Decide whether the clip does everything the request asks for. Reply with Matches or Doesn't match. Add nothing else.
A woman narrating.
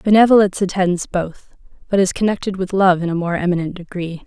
Matches